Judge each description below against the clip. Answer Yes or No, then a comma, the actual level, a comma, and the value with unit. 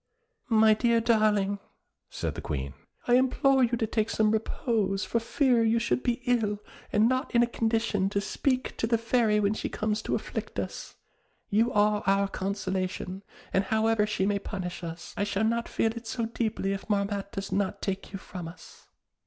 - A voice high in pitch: Yes, high, 215 Hz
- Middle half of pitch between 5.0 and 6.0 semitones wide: No, average, 2.7 semitones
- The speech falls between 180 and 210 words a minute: Yes, average, 185 wpm